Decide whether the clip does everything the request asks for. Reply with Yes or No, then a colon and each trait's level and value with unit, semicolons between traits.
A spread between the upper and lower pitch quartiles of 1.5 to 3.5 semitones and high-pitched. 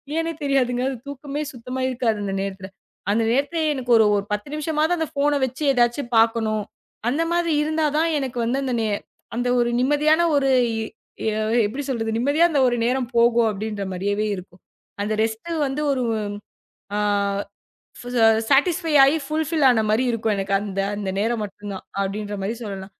No: average, 5.2 semitones; high, 245 Hz